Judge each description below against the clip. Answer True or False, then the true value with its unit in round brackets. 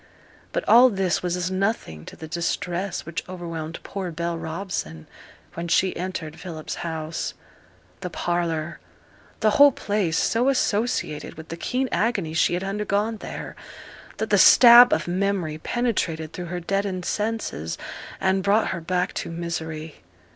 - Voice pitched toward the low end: False (180 Hz)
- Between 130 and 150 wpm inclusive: True (145 wpm)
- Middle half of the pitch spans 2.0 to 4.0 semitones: True (3.7 semitones)